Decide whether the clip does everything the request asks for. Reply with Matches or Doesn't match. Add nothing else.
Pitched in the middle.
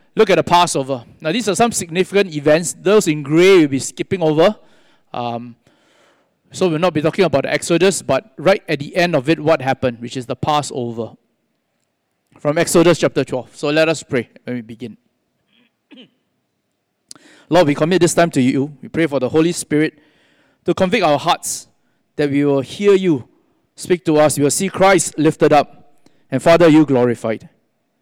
Matches